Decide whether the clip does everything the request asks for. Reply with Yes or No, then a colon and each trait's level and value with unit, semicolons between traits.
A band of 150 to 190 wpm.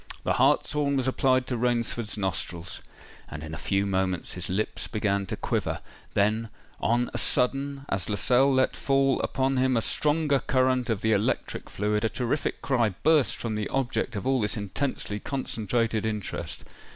Yes: average, 165 wpm